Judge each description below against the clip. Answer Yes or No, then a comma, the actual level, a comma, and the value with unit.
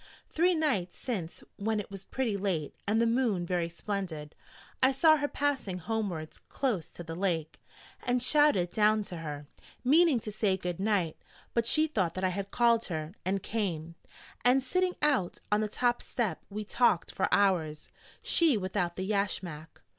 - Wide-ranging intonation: Yes, wide, 5.7 semitones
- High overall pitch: Yes, high, 200 Hz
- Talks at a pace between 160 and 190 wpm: Yes, average, 170 wpm